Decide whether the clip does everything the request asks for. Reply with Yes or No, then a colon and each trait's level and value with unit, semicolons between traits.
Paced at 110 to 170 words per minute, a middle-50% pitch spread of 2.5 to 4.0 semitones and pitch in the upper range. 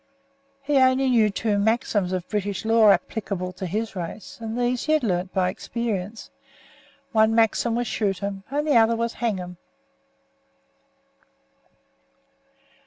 Yes: average, 140 wpm; average, 3.4 semitones; high, 220 Hz